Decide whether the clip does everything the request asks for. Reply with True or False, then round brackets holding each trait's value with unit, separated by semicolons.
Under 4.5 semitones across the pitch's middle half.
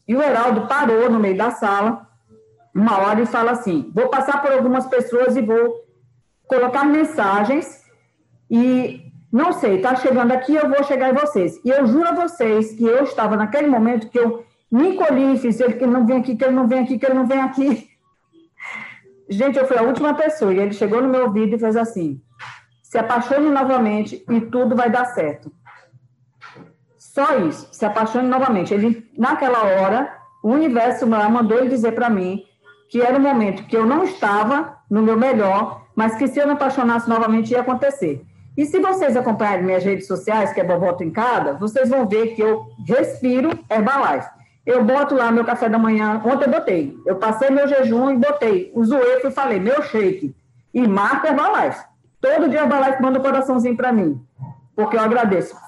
True (3.9 semitones)